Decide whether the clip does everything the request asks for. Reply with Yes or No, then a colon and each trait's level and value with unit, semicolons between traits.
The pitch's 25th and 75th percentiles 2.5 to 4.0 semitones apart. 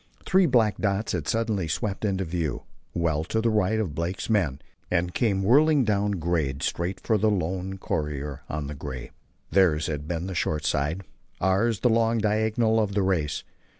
No: wide, 5.5 semitones